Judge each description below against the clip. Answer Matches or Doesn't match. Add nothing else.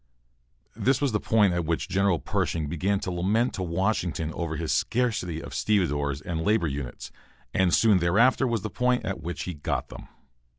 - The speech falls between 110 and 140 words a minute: Doesn't match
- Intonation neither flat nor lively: Matches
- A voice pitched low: Matches